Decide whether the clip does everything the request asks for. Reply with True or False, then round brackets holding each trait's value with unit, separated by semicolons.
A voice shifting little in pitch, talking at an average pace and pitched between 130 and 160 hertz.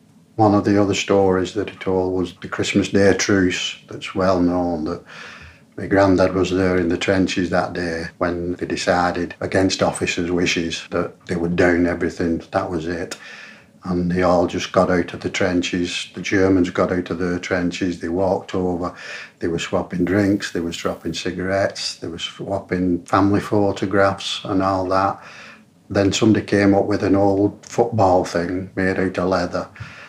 False (1.8 semitones; 175 wpm; 95 Hz)